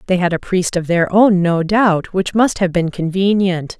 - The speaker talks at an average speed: No, fast, 220 wpm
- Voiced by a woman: Yes, female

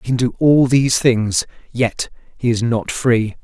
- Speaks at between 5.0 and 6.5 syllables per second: No, 4.3 syllables/s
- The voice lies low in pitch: Yes, low, 120 Hz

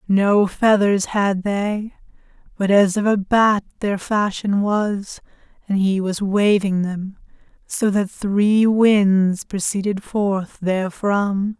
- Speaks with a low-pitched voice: No, high, 200 Hz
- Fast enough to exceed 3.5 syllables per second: No, 3.2 syllables/s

